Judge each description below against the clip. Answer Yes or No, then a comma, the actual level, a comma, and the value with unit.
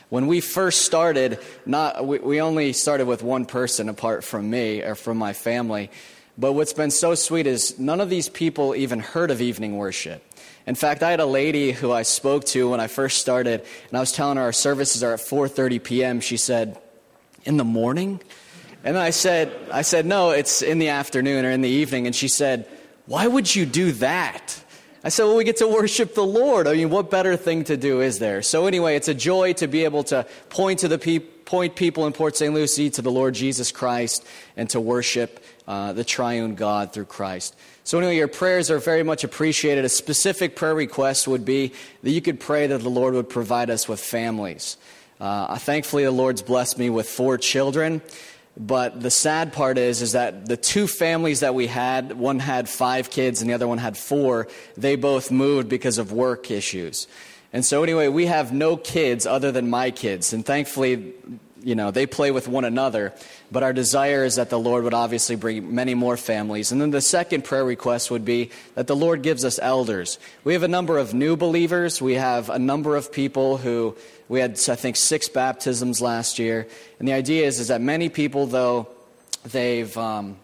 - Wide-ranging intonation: No, average, 4.2 semitones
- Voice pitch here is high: No, low, 130 Hz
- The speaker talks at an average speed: No, fast, 210 wpm